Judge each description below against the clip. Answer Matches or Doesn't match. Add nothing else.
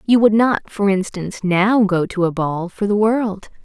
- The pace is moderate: Doesn't match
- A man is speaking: Doesn't match